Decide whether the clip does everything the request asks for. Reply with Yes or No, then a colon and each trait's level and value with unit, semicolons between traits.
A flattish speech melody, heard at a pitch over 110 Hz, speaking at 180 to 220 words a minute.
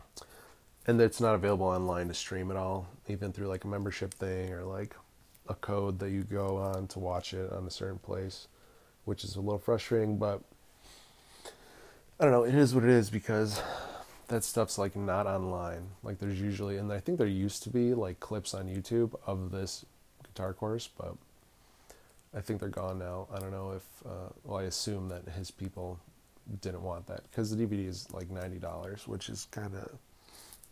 No: narrow, 2.3 semitones; low, 100 Hz; average, 190 wpm